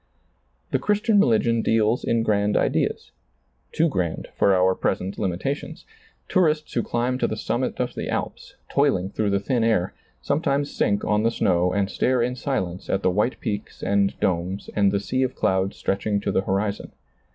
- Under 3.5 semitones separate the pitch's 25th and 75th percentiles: No, average, 4.7 semitones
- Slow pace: No, average, 175 wpm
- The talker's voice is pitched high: No, low, 105 Hz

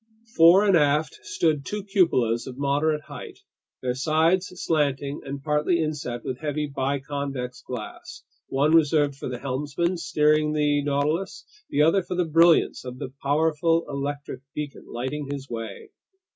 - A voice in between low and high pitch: Yes, medium, 150 Hz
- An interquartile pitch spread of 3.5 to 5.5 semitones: No, average, 2.7 semitones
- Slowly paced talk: No, average, 145 wpm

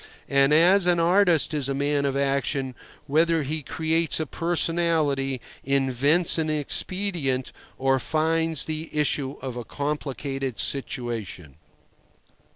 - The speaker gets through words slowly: Yes, slow, 115 wpm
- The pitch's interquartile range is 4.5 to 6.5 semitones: No, average, 3.2 semitones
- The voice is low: No, medium, 145 Hz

